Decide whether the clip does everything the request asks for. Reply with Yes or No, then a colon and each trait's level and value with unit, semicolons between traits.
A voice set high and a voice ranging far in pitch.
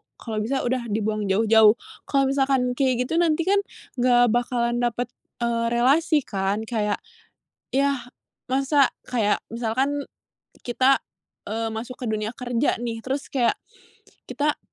No: high, 245 Hz; average, 3.2 semitones